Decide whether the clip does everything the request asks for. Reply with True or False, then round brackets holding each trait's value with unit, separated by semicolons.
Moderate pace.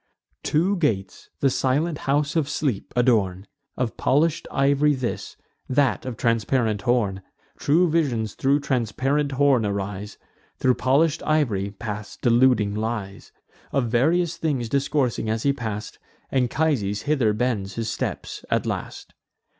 False (130 wpm)